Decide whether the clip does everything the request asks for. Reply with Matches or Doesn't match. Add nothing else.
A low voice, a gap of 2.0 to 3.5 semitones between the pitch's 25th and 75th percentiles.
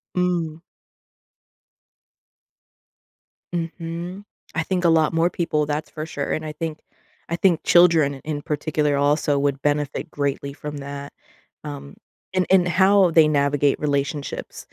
Doesn't match